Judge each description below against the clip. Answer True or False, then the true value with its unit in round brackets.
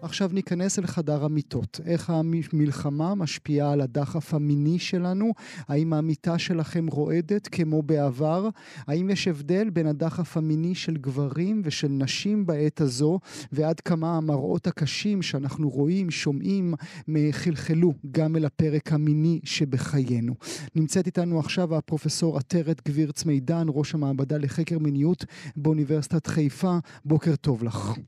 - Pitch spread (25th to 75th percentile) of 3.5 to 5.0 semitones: False (2.4 semitones)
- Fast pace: False (125 wpm)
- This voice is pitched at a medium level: True (155 Hz)